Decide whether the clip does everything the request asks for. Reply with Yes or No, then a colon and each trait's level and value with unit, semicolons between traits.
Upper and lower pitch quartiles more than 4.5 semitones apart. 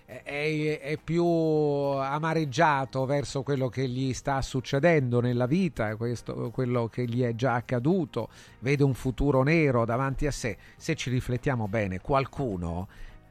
No: average, 3.2 semitones